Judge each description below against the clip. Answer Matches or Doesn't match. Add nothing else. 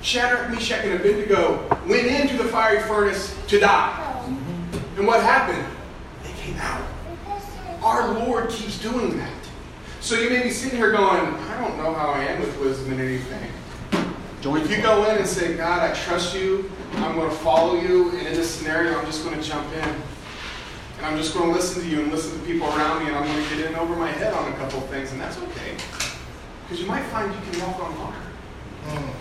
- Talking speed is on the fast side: Matches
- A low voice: Doesn't match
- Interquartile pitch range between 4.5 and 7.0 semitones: Matches